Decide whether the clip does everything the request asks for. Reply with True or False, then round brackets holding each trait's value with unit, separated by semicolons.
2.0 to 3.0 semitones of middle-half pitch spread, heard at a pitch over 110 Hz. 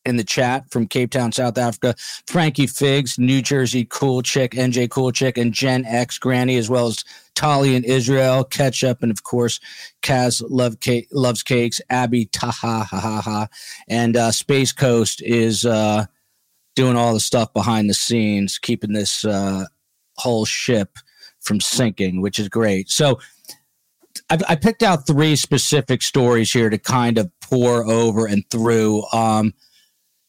True (2.6 semitones; 120 Hz)